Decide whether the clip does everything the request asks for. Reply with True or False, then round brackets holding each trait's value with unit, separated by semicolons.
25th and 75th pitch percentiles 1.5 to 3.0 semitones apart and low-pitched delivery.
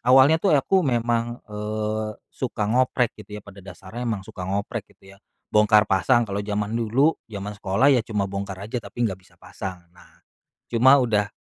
False (3.6 semitones; 105 Hz)